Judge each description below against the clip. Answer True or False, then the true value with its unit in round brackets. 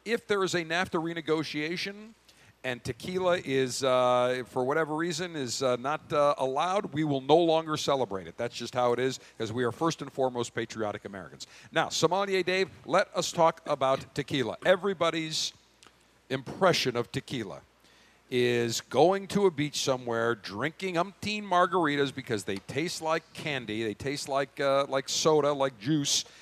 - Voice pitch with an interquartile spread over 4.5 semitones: True (5.0 semitones)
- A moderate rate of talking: True (160 wpm)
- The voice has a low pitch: False (145 Hz)